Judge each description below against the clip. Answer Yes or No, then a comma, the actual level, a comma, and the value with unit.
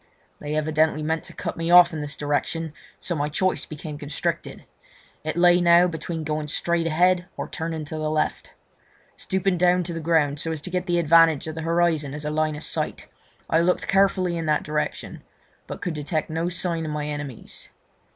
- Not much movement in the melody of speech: Yes, narrow, 2.2 semitones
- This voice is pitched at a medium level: Yes, medium, 160 Hz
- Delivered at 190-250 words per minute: Yes, average, 200 wpm